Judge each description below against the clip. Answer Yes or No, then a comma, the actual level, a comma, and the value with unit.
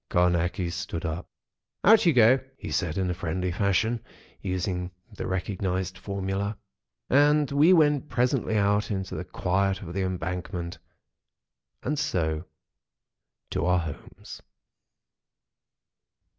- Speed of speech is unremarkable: No, slow, 115 wpm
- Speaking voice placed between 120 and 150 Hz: No, very low, 95 Hz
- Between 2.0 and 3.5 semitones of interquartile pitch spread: No, average, 3.9 semitones